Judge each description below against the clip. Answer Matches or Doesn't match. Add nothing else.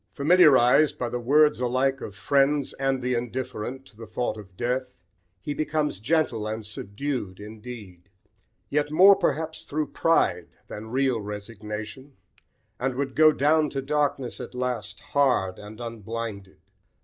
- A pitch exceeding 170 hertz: Doesn't match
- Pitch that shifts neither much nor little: Matches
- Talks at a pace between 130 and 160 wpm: Matches